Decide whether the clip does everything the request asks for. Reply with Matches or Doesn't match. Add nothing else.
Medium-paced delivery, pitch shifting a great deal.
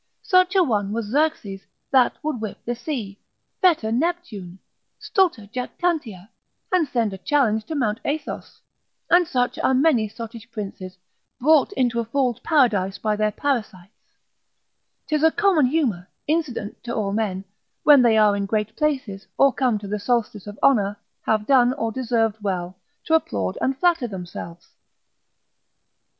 Matches